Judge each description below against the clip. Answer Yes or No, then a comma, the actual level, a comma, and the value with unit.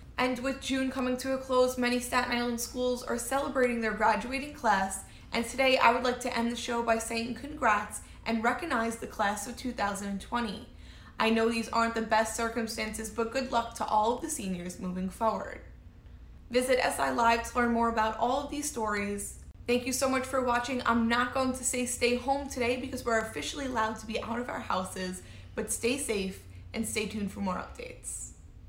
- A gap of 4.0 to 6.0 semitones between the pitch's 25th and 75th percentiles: No, narrow, 2.5 semitones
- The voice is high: Yes, high, 235 Hz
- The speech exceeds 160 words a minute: Yes, average, 200 wpm